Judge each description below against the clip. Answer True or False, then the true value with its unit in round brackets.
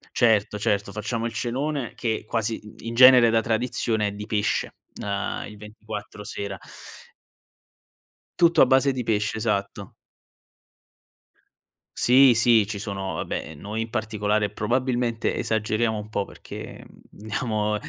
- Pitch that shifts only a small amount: True (2.2 semitones)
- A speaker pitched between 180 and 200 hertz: False (110 Hz)